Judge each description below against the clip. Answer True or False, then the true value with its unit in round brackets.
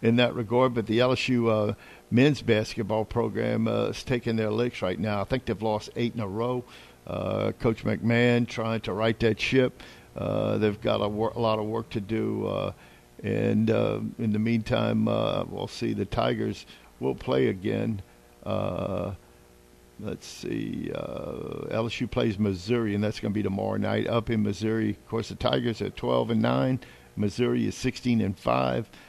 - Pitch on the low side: True (110 Hz)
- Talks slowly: False (180 wpm)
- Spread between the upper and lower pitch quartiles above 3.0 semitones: False (2.5 semitones)